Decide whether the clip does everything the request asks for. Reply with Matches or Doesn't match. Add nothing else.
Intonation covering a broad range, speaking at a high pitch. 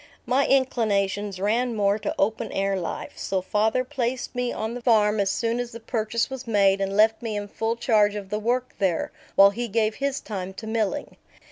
Doesn't match